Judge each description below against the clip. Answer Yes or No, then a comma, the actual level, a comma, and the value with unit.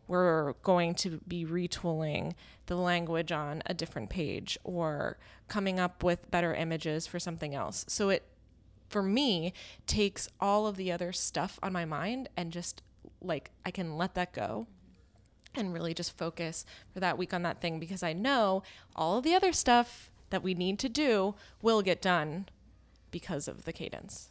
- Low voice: No, medium, 175 Hz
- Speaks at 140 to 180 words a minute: Yes, average, 175 wpm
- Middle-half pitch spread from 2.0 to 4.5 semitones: Yes, average, 2.7 semitones